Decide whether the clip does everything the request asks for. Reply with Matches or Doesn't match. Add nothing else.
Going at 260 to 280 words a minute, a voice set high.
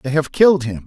Doesn't match